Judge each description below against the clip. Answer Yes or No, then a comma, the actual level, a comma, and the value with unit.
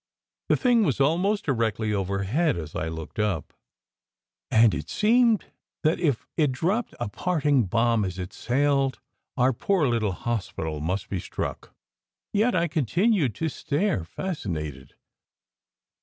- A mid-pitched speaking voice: No, low, 125 Hz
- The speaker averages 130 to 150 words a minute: Yes, slow, 135 wpm